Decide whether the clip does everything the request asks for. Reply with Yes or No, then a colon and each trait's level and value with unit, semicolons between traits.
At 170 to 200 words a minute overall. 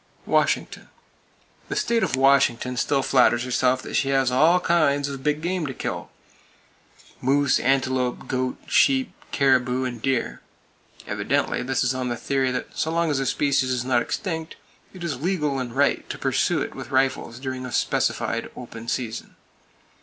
No: average, 160 wpm